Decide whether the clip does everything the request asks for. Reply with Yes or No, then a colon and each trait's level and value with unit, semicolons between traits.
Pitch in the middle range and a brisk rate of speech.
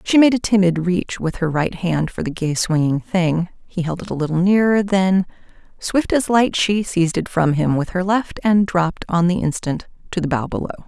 Yes: medium, 180 Hz; fast, 215 wpm